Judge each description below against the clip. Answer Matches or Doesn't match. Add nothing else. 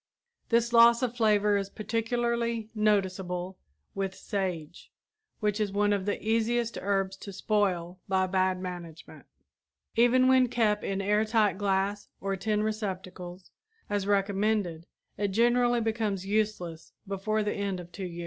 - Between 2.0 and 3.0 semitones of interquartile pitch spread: Matches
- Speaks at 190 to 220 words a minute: Doesn't match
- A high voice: Matches